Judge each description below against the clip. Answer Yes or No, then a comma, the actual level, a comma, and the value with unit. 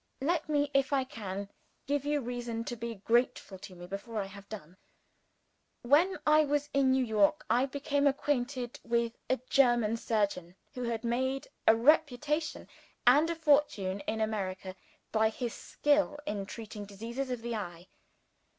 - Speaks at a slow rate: No, average, 160 wpm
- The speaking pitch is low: No, high, 240 Hz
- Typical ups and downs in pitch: Yes, average, 5.0 semitones